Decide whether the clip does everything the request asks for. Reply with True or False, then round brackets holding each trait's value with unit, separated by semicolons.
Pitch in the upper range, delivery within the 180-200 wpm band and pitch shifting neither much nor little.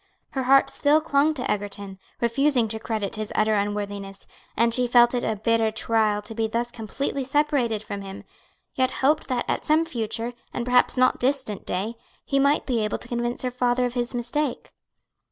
True (240 Hz; 190 wpm; 3.3 semitones)